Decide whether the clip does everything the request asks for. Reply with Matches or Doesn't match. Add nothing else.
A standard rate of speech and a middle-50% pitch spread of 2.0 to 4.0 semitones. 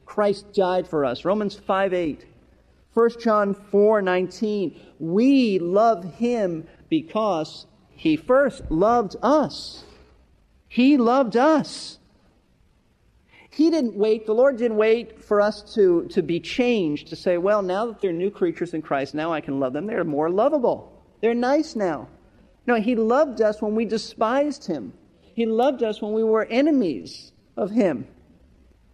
Doesn't match